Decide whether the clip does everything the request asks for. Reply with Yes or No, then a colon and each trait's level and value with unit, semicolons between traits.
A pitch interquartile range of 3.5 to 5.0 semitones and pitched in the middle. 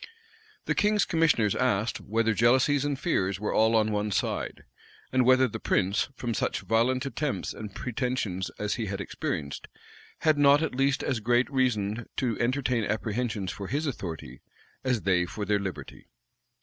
No: average, 4.3 semitones; low, 115 Hz